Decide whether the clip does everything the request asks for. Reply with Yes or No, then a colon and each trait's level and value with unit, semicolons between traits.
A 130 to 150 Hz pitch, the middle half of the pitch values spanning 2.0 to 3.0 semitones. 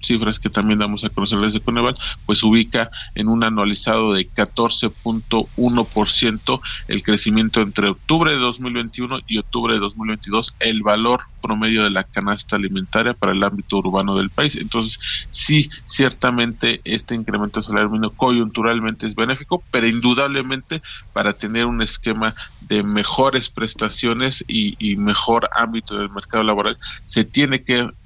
No: low, 110 Hz; narrow, 2.4 semitones